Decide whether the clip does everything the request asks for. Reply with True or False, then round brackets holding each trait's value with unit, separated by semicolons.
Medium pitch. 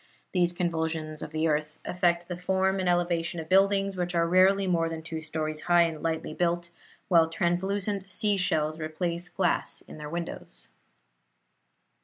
True (175 Hz)